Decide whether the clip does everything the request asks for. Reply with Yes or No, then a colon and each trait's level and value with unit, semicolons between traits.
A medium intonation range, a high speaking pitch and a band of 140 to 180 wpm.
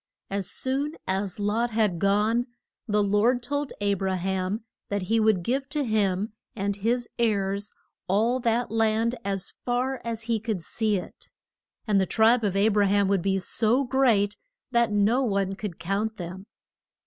Yes: average, 3.0 semitones; high, 210 Hz; average, 170 wpm